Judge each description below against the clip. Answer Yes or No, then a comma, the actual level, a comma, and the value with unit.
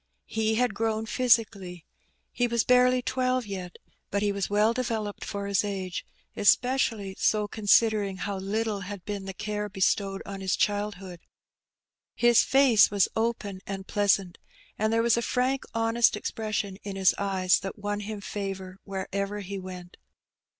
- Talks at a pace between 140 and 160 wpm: Yes, average, 155 wpm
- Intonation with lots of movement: No, narrow, 2.6 semitones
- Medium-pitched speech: No, high, 205 Hz